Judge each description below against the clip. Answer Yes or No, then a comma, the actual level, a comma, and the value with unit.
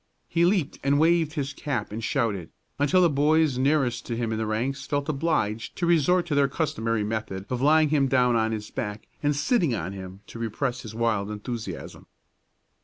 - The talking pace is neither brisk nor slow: Yes, average, 190 wpm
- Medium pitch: No, low, 130 Hz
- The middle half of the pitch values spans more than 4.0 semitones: Yes, average, 5.3 semitones